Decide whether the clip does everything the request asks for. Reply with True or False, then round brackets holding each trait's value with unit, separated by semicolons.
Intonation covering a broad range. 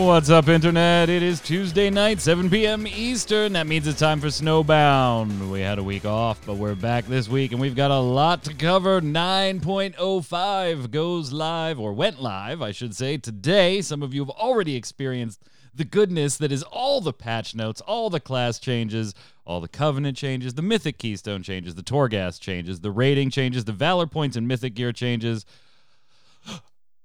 True (6.2 semitones)